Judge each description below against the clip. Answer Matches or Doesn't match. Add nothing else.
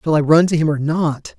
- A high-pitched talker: Doesn't match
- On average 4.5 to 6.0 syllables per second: Matches